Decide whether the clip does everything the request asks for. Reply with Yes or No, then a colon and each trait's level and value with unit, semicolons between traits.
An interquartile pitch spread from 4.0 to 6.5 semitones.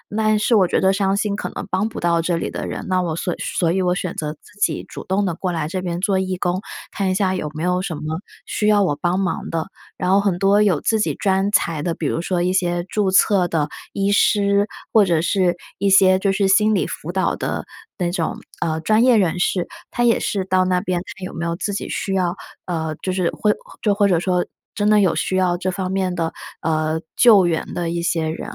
No: narrow, 2.5 semitones